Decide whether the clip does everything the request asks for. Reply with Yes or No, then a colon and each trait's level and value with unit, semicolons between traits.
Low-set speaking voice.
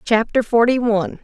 No: high, 230 Hz